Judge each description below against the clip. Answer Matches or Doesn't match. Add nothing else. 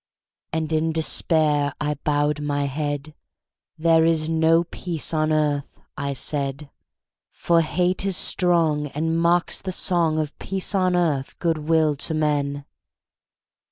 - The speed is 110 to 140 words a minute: Matches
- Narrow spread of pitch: Matches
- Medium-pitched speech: Matches